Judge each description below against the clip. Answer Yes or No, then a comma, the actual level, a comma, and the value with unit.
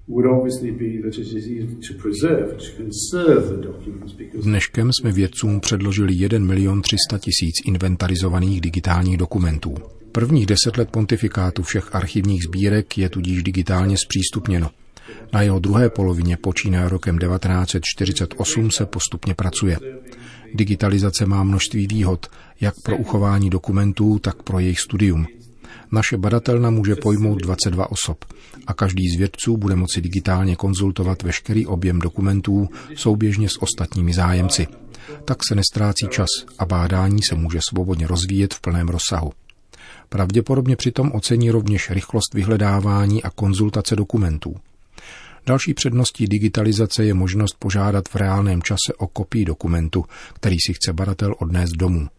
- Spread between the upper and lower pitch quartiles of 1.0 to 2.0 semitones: No, average, 2.9 semitones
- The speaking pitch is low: Yes, low, 100 Hz